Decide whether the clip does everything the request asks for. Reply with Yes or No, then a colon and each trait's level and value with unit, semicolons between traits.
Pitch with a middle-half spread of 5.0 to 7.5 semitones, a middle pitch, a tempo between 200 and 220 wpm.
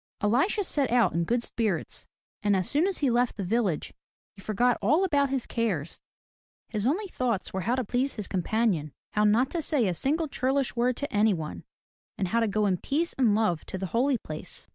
No: average, 5.3 semitones; high, 230 Hz; fast, 205 wpm